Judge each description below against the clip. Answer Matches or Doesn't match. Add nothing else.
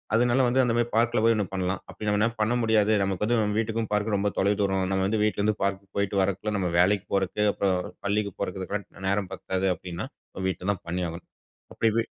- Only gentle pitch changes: Matches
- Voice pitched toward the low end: Matches